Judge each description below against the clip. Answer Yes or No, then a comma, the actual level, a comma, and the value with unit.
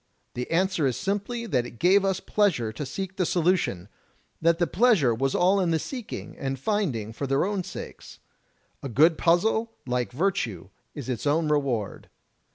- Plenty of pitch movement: Yes, wide, 7.2 semitones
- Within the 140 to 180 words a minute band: Yes, average, 175 wpm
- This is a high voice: No, medium, 165 Hz